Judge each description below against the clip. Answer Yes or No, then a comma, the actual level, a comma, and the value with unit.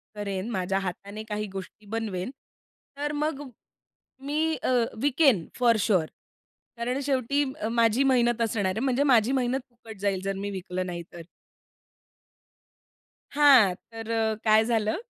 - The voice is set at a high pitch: Yes, high, 225 Hz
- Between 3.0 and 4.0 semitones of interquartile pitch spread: No, average, 4.7 semitones